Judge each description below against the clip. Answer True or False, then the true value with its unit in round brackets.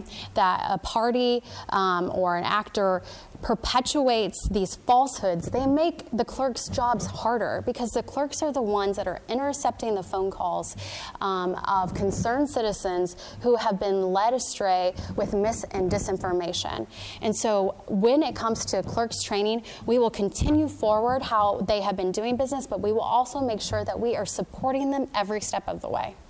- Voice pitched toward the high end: True (215 Hz)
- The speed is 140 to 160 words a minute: False (170 wpm)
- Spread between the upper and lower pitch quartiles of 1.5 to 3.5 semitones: False (4.2 semitones)